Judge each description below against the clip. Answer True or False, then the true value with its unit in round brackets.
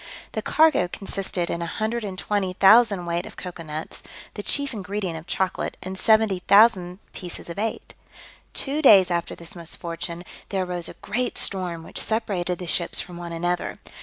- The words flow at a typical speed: True (155 wpm)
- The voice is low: False (185 Hz)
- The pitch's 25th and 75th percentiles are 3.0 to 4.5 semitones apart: True (3.3 semitones)